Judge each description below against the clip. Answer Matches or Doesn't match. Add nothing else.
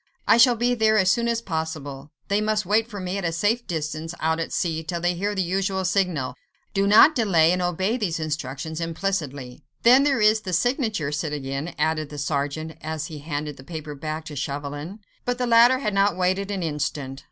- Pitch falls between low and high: Matches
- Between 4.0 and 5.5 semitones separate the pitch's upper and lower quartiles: Matches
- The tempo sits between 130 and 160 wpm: Doesn't match